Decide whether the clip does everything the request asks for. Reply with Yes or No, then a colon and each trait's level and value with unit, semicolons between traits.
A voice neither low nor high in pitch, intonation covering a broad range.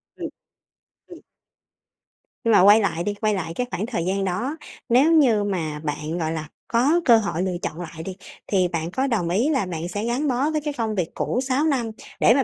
No: high, 205 Hz; wide, 6.3 semitones